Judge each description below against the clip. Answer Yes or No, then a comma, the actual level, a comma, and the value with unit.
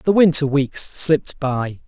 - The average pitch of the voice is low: No, medium, 145 Hz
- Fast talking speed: No, average, 160 wpm